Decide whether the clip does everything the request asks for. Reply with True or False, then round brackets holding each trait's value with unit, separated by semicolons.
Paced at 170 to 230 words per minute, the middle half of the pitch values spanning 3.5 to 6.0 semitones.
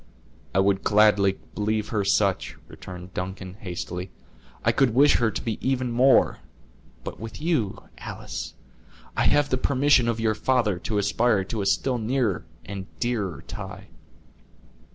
False (150 wpm; 4.2 semitones)